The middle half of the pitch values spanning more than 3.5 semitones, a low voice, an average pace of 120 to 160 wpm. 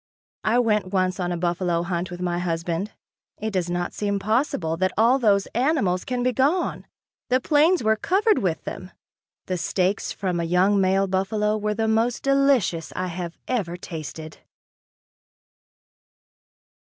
No: average, 4.4 semitones; high, 195 Hz; average, 155 wpm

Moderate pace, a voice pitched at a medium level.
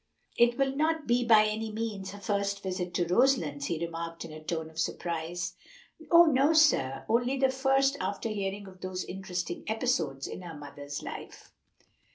No: average, 175 wpm; high, 200 Hz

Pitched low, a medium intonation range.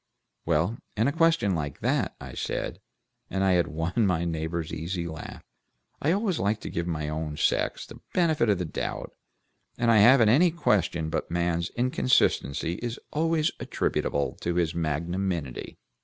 No: very low, 90 Hz; wide, 6.6 semitones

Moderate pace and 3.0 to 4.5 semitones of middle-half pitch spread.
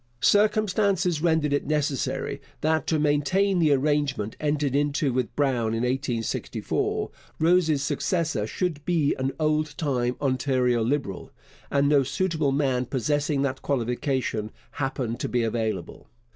No: slow, 130 wpm; average, 3.4 semitones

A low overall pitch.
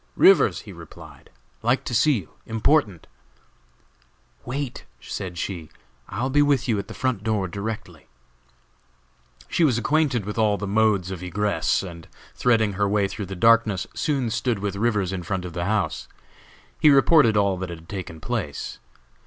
Yes: low, 105 Hz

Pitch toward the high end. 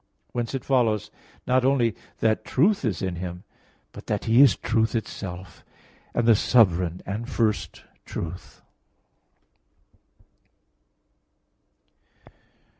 No: low, 110 Hz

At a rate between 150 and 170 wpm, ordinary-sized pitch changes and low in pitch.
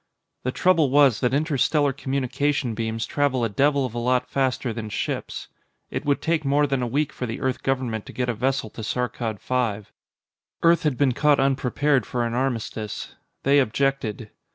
No: average, 180 wpm; average, 3.2 semitones; low, 130 Hz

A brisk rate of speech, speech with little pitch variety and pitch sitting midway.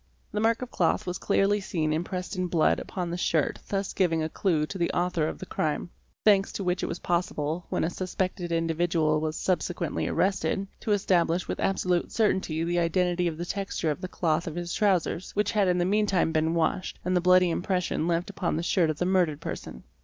Yes: fast, 215 wpm; narrow, 2.3 semitones; medium, 175 Hz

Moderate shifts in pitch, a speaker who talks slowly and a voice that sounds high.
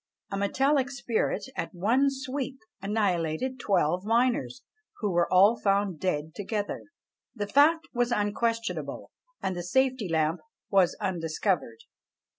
No: wide, 5.8 semitones; slow, 120 wpm; high, 205 Hz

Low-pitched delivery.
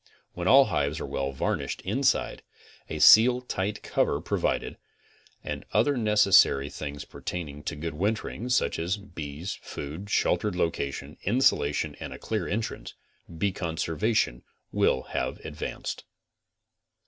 Yes: very low, 90 Hz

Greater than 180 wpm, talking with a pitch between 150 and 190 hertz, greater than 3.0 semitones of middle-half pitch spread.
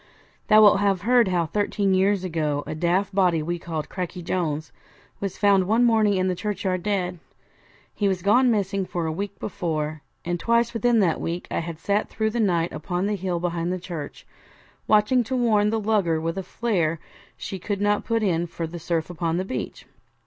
Yes: average, 200 wpm; medium, 185 Hz; average, 3.5 semitones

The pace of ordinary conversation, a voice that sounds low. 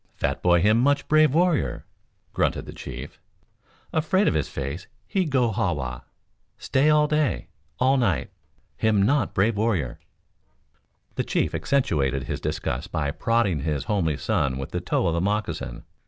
Yes: average, 155 wpm; low, 100 Hz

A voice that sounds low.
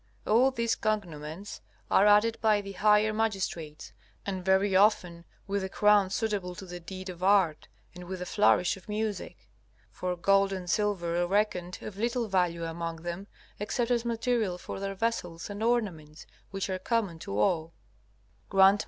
No: high, 195 Hz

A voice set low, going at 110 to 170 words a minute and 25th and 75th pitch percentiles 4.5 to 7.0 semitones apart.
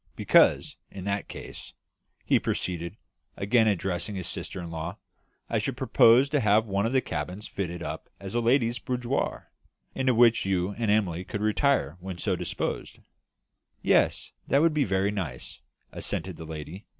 Yes: low, 100 Hz; average, 160 wpm; average, 4.8 semitones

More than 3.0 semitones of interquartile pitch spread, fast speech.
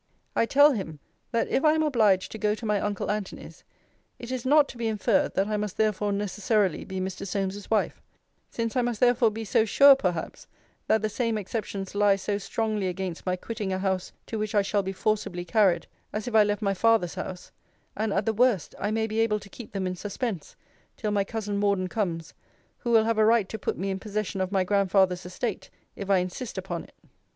No: average, 2.7 semitones; fast, 215 wpm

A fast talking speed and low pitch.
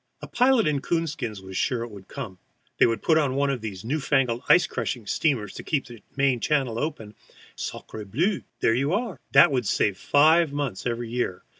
Yes: fast, 210 wpm; low, 130 Hz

